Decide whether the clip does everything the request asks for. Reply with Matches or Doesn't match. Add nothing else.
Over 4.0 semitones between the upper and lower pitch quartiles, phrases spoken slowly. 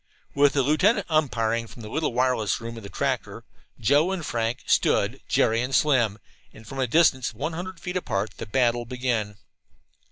Doesn't match